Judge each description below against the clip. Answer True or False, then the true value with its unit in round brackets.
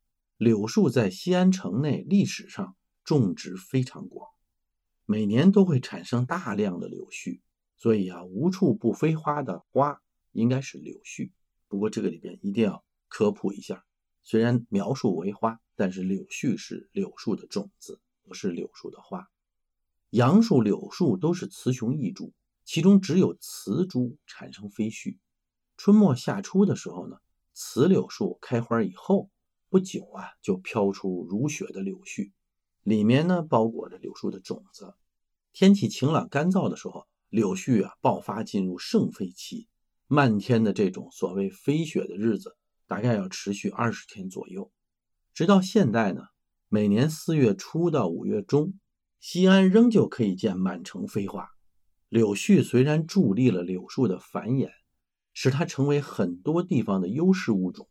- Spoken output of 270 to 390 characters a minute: False (230 characters per minute)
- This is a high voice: False (135 Hz)